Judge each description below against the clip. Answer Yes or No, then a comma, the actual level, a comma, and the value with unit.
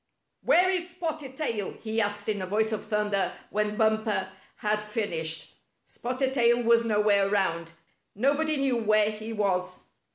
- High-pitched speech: Yes, high, 215 Hz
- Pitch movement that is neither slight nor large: Yes, average, 3.0 semitones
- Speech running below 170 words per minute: Yes, average, 150 wpm